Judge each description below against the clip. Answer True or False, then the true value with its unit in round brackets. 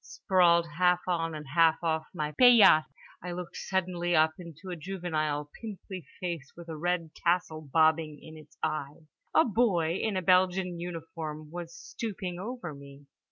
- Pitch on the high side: False (170 Hz)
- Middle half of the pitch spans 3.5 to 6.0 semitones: False (2.5 semitones)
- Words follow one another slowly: False (160 wpm)